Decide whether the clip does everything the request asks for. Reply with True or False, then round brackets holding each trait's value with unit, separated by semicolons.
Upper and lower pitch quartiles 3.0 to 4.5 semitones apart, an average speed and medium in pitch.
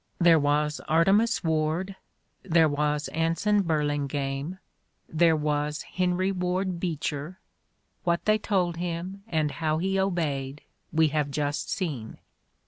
False (3.5 semitones; 125 wpm; 160 Hz)